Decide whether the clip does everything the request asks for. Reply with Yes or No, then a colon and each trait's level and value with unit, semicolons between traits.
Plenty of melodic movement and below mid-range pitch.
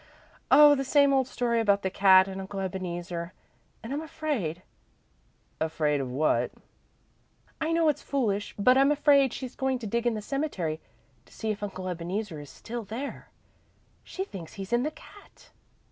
No: wide, 6.6 semitones; high, 220 Hz